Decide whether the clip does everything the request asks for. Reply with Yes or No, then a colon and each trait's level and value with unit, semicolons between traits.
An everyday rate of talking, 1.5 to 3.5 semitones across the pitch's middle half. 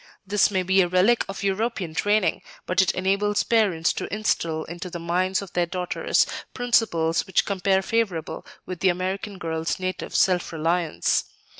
Yes: average, 160 wpm; narrow, 2.5 semitones